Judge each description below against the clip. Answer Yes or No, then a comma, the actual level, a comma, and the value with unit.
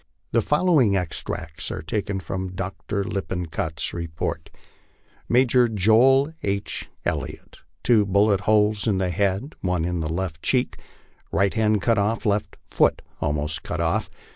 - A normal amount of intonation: Yes, average, 3.6 semitones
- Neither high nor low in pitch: No, low, 100 Hz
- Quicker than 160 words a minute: No, slow, 135 wpm